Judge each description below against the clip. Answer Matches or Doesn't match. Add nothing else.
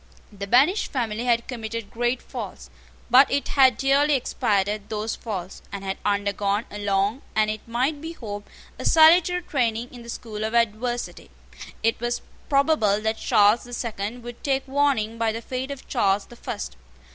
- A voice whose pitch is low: Doesn't match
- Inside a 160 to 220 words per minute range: Matches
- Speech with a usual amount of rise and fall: Matches